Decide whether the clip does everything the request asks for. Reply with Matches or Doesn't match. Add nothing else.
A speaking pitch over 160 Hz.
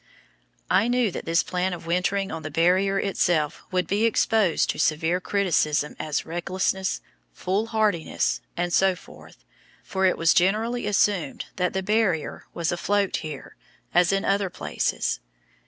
Matches